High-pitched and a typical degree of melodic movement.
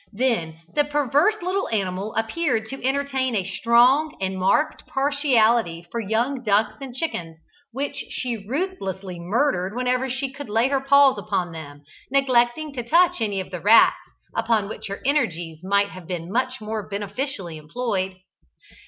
No: high, 230 Hz; wide, 5.9 semitones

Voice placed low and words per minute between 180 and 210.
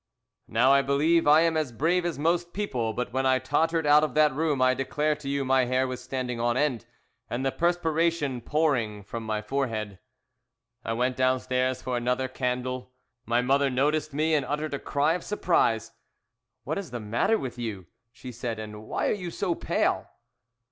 Yes: low, 130 Hz; average, 190 wpm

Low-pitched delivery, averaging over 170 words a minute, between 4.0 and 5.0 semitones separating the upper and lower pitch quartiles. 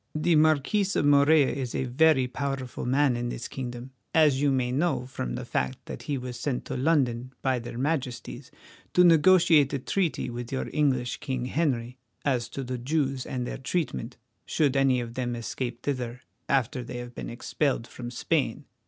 No: low, 130 Hz; average, 180 wpm; average, 3.0 semitones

